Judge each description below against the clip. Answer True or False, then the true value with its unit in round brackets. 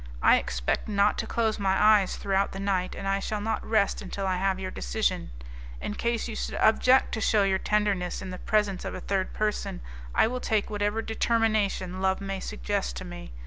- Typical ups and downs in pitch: False (2.2 semitones)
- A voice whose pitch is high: True (200 Hz)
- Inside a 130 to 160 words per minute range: False (205 wpm)